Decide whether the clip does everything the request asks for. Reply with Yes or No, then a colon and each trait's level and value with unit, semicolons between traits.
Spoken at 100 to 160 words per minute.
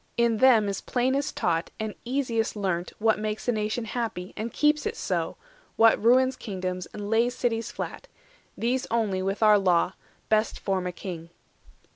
No: average, 170 wpm